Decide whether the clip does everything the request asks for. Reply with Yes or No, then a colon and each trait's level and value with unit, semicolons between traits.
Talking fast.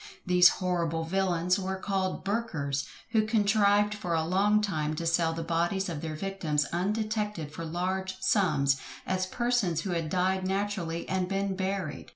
No: average, 160 wpm